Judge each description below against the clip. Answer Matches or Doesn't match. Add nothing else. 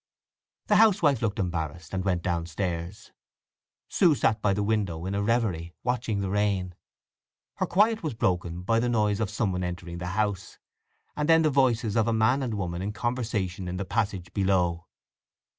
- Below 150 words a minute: Doesn't match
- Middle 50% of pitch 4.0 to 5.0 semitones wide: Matches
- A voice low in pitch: Matches